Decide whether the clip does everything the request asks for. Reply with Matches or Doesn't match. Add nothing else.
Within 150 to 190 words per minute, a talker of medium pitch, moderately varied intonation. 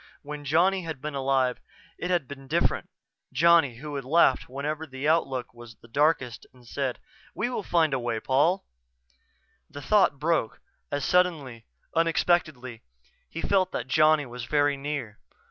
Matches